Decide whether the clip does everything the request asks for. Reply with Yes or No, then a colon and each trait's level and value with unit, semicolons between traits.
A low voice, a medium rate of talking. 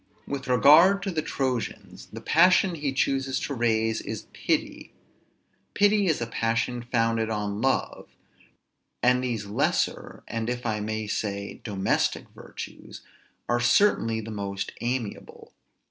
No: low, 120 Hz; slow, 130 wpm